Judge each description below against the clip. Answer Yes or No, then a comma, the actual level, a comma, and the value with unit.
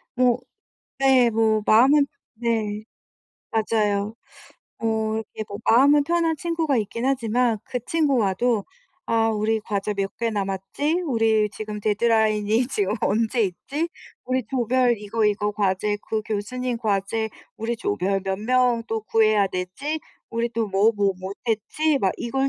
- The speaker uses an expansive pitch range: No, average, 3.2 semitones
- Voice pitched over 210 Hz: Yes, high, 225 Hz